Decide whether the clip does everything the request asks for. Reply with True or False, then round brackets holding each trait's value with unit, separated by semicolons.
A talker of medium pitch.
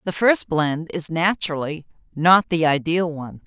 True (165 Hz)